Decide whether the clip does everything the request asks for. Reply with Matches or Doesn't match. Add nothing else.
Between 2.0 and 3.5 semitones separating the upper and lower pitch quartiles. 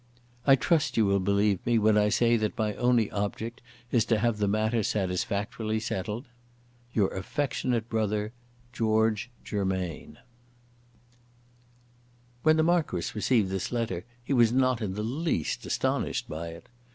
Matches